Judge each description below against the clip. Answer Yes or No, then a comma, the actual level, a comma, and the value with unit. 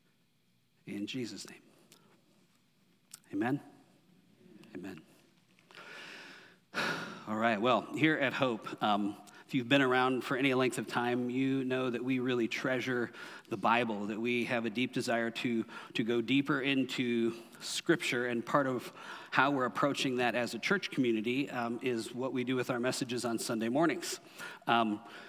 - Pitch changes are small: Yes, narrow, 2.1 semitones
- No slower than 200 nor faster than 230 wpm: No, average, 150 wpm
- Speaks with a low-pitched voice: Yes, low, 125 Hz